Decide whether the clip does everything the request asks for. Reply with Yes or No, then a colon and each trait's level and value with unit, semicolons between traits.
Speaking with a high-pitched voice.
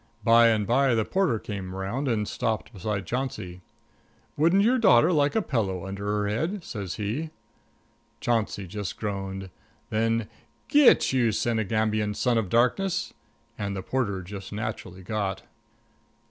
No: low, 110 Hz